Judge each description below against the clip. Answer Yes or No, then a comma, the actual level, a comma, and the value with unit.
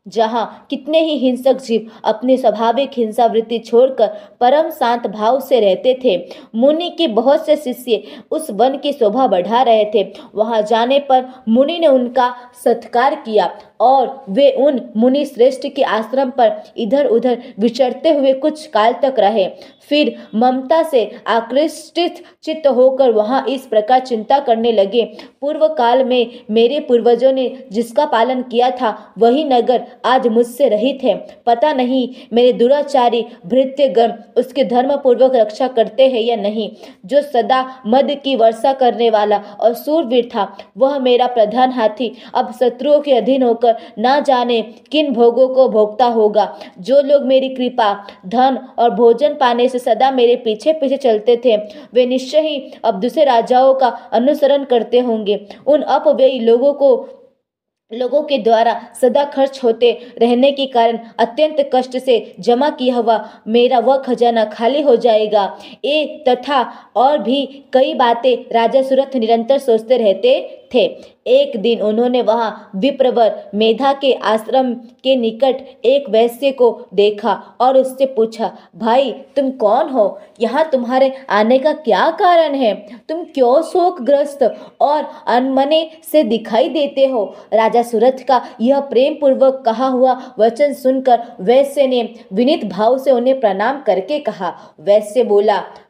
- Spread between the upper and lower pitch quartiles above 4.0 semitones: No, average, 3.1 semitones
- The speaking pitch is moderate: No, very high, 250 Hz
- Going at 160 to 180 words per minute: No, average, 150 wpm